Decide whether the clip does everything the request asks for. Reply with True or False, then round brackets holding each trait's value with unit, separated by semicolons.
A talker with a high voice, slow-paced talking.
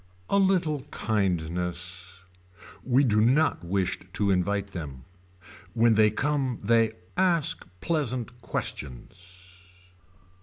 False (105 Hz; 100 wpm)